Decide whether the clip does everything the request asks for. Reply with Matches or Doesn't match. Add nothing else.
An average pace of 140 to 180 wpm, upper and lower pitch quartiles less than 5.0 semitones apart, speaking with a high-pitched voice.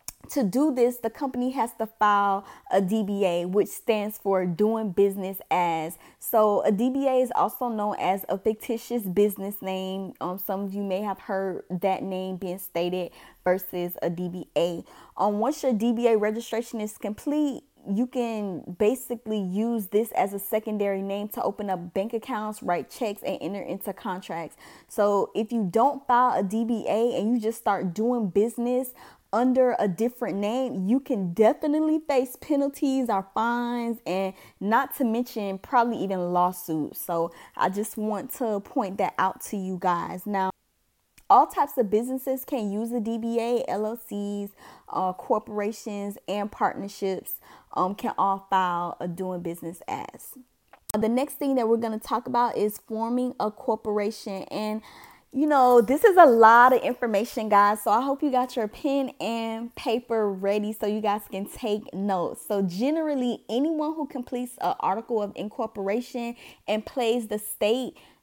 Matches